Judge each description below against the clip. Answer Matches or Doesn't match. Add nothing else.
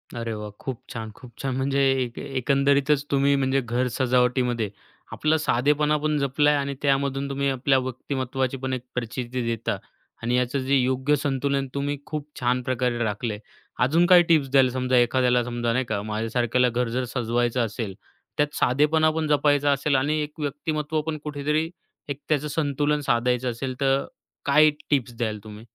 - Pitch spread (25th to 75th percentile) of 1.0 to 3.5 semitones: Matches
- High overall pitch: Doesn't match